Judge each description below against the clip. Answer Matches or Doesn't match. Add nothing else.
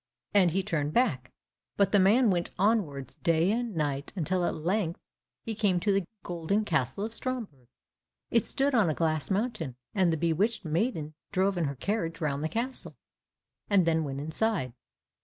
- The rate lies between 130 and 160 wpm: Doesn't match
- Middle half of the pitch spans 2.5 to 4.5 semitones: Doesn't match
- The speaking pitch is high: Doesn't match